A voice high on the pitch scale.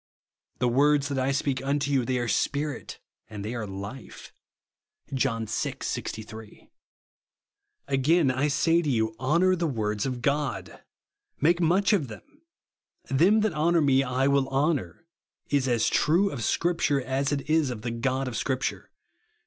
No: low, 135 Hz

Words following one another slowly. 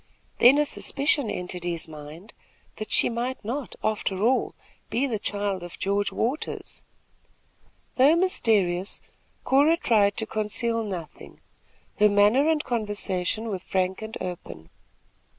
Yes: slow, 130 wpm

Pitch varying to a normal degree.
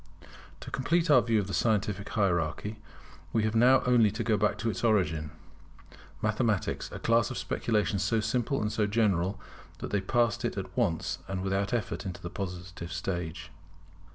Yes: average, 3.5 semitones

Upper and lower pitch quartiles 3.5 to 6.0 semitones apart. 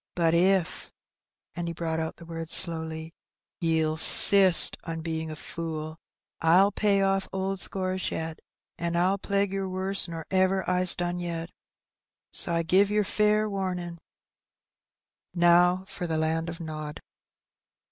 No: average, 2.7 semitones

